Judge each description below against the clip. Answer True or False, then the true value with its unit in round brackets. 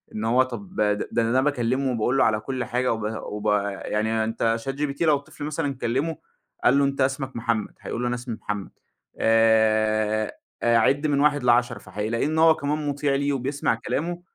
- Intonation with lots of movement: False (4.0 semitones)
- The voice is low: True (125 Hz)